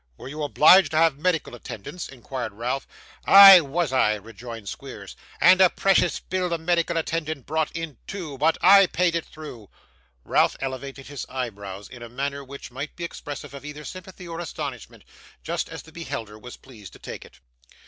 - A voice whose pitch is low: No, medium, 145 Hz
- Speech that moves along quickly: No, average, 180 wpm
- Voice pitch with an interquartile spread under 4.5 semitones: No, average, 5.2 semitones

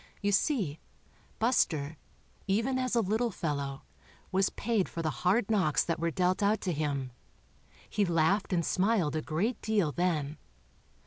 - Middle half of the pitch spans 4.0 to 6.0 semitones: Yes, wide, 5.5 semitones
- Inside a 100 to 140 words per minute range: No, average, 150 wpm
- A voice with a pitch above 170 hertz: Yes, medium, 185 Hz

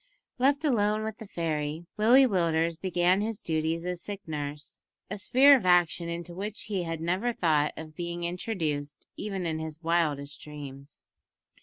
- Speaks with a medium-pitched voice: Yes, medium, 170 Hz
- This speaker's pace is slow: No, average, 160 wpm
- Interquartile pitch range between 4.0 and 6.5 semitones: Yes, average, 4.4 semitones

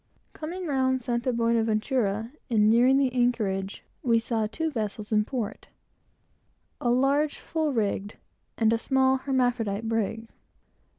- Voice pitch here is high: Yes, high, 235 Hz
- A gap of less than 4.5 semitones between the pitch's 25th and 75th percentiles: Yes, average, 3.1 semitones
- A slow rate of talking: Yes, slow, 125 wpm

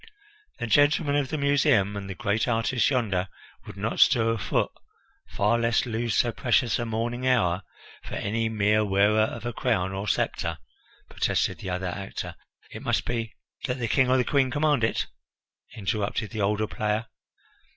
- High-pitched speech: No, low, 115 Hz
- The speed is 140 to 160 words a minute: No, average, 175 wpm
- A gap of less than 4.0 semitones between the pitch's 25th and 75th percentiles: Yes, average, 3.2 semitones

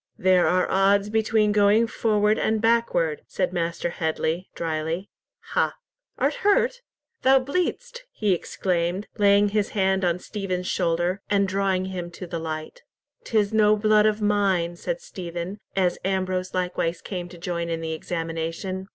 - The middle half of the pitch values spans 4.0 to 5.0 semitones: No, average, 3.4 semitones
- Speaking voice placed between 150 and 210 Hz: Yes, high, 190 Hz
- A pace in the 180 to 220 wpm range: No, average, 150 wpm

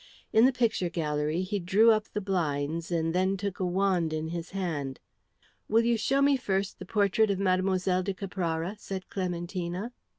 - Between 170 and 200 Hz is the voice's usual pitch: Yes, medium, 185 Hz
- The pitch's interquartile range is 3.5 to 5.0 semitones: No, average, 3.0 semitones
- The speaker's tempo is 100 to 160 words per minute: No, average, 175 wpm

